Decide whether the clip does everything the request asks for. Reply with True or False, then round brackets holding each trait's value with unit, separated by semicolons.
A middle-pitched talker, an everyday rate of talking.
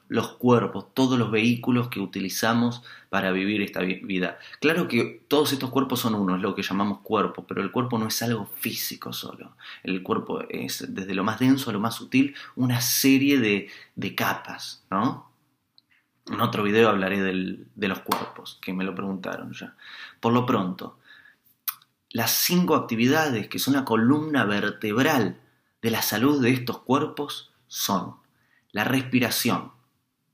False (115 Hz; 160 wpm)